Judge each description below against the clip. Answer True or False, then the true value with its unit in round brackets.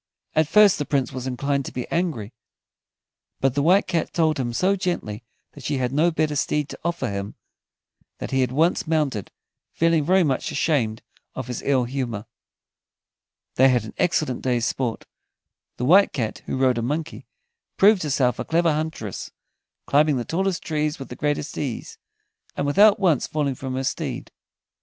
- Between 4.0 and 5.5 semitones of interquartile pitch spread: True (4.5 semitones)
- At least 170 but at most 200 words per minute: True (175 wpm)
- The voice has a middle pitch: True (145 Hz)